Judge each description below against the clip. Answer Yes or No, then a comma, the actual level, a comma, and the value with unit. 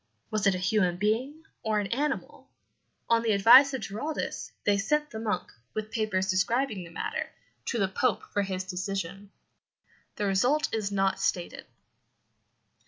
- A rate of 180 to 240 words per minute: No, average, 155 wpm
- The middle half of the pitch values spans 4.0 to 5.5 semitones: No, average, 3.4 semitones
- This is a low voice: No, high, 210 Hz